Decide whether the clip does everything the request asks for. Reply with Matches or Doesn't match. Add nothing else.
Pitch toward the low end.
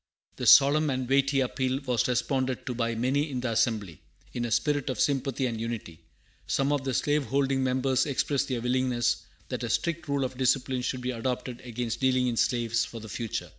Matches